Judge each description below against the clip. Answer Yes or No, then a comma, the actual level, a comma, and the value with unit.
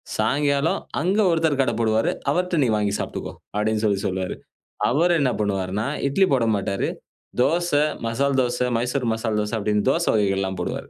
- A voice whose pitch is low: Yes, low, 115 Hz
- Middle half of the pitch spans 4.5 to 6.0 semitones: Yes, average, 5.3 semitones